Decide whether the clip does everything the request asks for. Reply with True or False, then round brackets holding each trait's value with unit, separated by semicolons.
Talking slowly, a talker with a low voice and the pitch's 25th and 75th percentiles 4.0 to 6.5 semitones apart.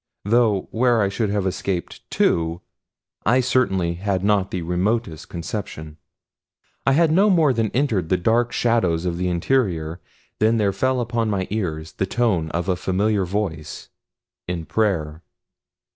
False (150 wpm; 100 Hz; 4.9 semitones)